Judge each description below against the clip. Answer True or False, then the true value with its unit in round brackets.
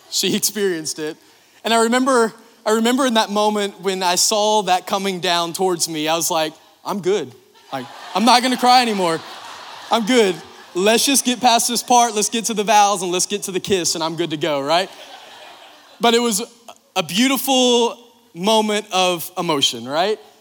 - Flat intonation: False (4.7 semitones)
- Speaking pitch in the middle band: False (210 Hz)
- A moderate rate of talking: True (190 wpm)